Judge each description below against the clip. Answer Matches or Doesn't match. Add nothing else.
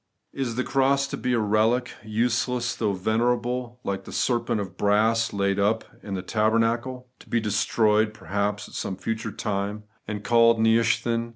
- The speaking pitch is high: Doesn't match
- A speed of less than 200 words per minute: Matches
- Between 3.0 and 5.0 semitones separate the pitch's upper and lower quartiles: Doesn't match